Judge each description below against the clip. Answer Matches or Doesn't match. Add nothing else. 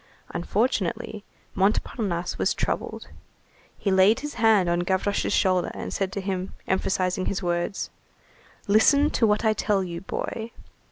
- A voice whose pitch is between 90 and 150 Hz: Doesn't match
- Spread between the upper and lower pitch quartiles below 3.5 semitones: Matches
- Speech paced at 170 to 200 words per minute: Doesn't match